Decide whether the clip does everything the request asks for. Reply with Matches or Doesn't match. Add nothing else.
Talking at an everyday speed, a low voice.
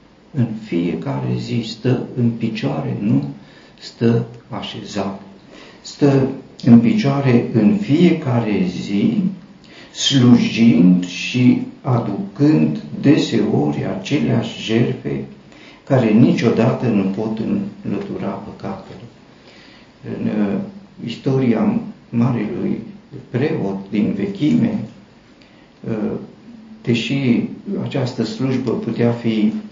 Doesn't match